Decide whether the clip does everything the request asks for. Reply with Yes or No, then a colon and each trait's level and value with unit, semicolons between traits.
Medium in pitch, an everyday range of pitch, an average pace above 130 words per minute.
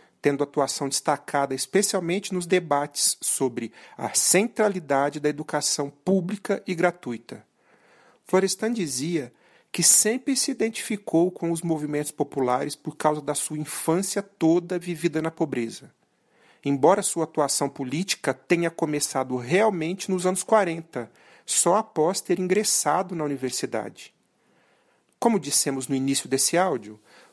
No: medium, 160 Hz; average, 4.6 semitones; slow, 120 wpm